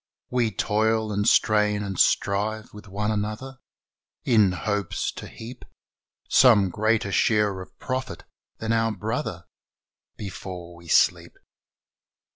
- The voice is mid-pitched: No, low, 105 Hz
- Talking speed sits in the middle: No, slow, 115 wpm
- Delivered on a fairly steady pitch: Yes, narrow, 2.1 semitones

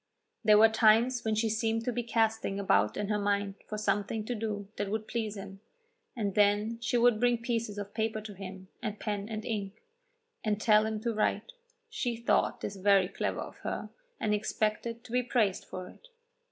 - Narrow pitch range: Yes, narrow, 2.0 semitones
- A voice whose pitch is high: Yes, high, 215 Hz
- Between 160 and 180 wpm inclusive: No, average, 195 wpm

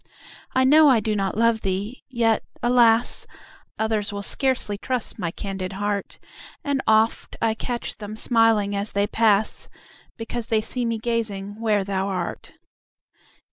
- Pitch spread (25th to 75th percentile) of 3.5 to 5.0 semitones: No, narrow, 2.4 semitones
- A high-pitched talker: Yes, high, 220 Hz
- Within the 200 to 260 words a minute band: No, average, 145 wpm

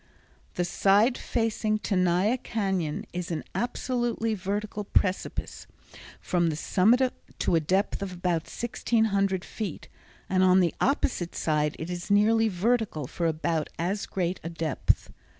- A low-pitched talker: No, high, 190 Hz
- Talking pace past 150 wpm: No, slow, 135 wpm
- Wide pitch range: No, average, 4.0 semitones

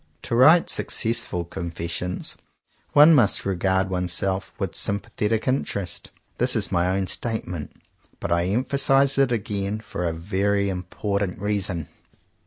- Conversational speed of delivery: No, slow, 130 wpm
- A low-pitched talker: Yes, low, 100 Hz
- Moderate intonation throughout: Yes, average, 3.8 semitones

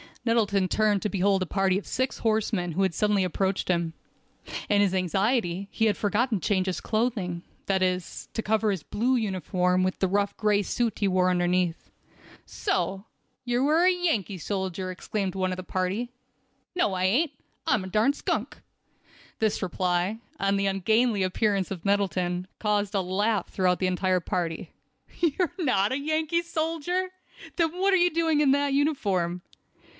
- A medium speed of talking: Yes, average, 170 wpm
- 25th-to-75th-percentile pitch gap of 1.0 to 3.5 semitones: No, average, 4.4 semitones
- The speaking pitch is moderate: No, high, 200 Hz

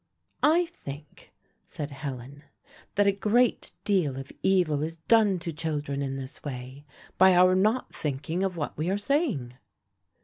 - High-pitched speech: No, medium, 160 Hz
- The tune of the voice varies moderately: No, wide, 5.7 semitones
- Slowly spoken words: No, average, 150 wpm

